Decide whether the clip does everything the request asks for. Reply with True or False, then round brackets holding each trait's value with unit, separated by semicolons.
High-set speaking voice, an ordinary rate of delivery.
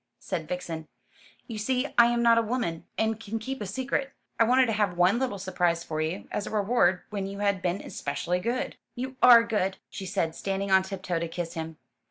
False (200 Hz; 215 wpm)